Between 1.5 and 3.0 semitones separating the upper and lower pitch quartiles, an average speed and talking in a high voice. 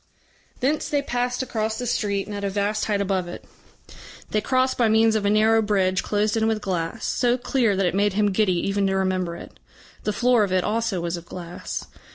No: average, 2.7 semitones; fast, 215 wpm; high, 210 Hz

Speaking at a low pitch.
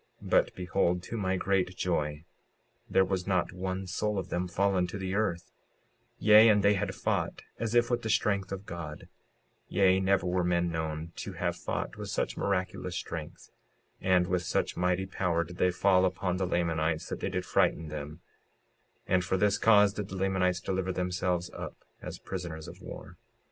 Yes: very low, 90 Hz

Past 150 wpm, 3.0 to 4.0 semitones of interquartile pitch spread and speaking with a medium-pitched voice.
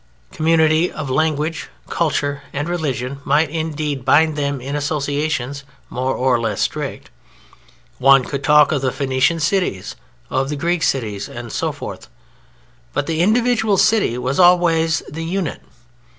No: average, 140 wpm; average, 3.4 semitones; medium, 150 Hz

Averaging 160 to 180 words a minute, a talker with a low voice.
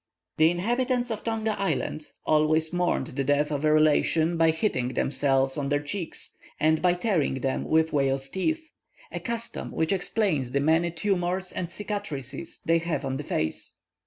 No: average, 165 wpm; medium, 160 Hz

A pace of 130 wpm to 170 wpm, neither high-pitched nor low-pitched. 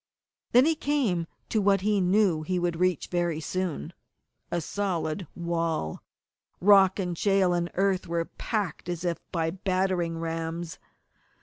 Yes: average, 145 wpm; medium, 180 Hz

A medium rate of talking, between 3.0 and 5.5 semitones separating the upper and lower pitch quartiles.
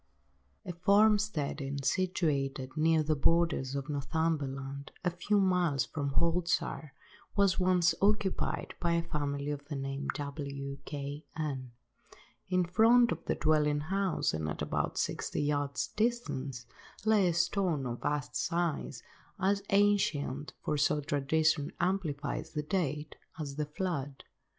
No: slow, 130 wpm; average, 4.3 semitones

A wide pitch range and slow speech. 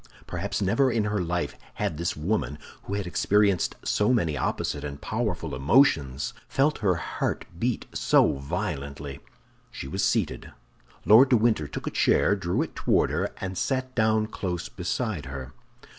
No: wide, 6.7 semitones; average, 160 wpm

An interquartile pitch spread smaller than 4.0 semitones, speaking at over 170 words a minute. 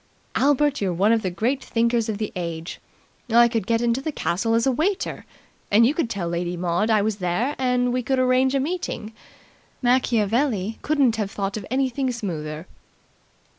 No: average, 4.5 semitones; average, 180 wpm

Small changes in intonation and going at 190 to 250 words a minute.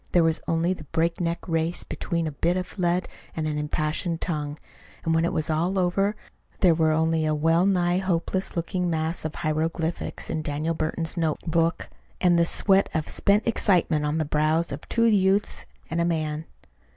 No: narrow, 2.1 semitones; average, 180 wpm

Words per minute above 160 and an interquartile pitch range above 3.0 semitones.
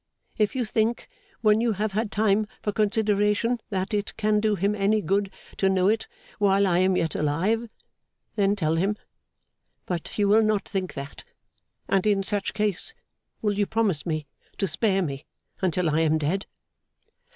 No: average, 170 wpm; narrow, 2.5 semitones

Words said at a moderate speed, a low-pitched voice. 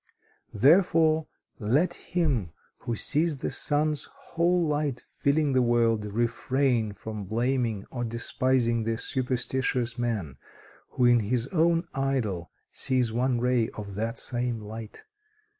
No: slow, 125 wpm; low, 125 Hz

